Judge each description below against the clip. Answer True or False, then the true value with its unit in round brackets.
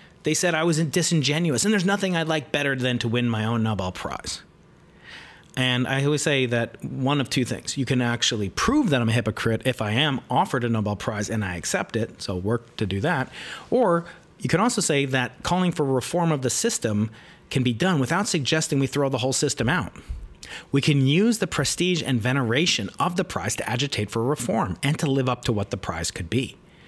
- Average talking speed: False (220 wpm)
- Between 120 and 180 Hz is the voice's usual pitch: True (135 Hz)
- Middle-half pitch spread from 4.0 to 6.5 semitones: True (5.1 semitones)